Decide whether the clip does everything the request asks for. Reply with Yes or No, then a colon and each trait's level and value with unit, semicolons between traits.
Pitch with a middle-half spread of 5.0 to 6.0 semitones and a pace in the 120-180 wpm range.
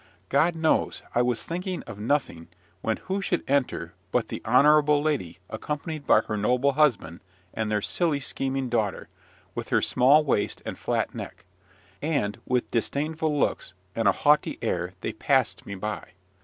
Yes: wide, 5.6 semitones; average, 160 wpm